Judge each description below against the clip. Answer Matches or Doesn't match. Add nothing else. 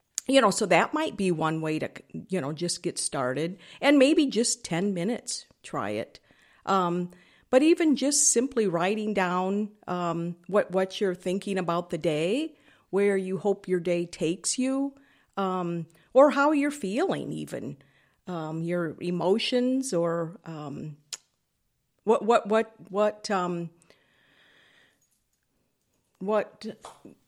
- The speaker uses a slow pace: Matches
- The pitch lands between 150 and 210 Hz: Matches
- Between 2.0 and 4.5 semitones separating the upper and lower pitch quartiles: Doesn't match